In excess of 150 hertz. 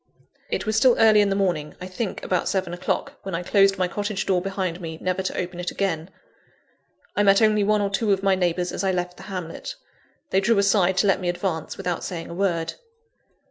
Yes: high, 190 Hz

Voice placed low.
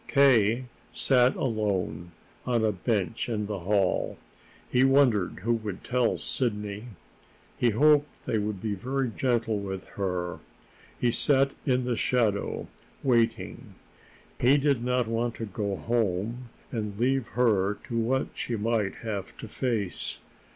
Yes: low, 115 Hz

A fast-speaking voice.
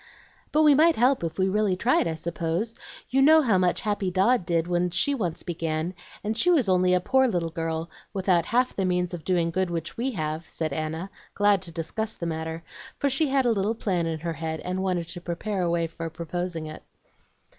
Yes: fast, 220 wpm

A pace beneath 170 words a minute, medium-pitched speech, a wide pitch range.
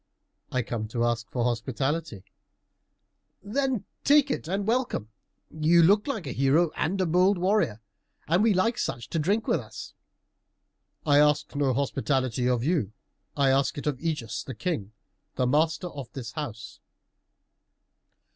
Yes: average, 150 wpm; medium, 150 Hz; wide, 6.6 semitones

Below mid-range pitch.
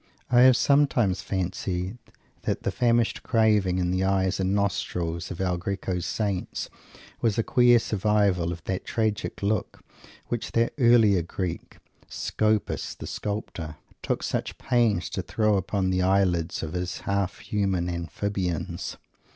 Yes: very low, 95 Hz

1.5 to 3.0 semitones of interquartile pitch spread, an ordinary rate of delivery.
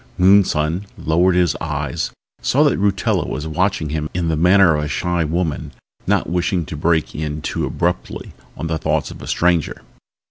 Yes: average, 2.7 semitones; average, 175 wpm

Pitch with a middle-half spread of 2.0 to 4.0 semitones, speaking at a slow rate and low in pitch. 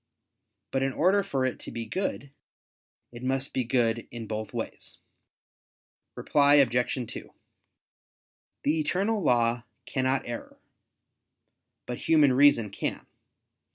Yes: average, 3.5 semitones; slow, 120 wpm; low, 130 Hz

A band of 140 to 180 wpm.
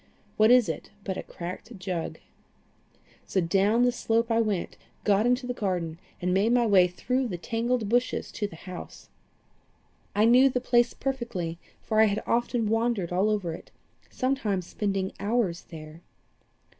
Yes: average, 160 wpm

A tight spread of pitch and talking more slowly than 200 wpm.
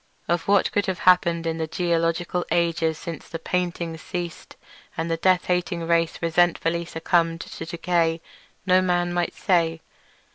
Yes: narrow, 1.3 semitones; average, 150 wpm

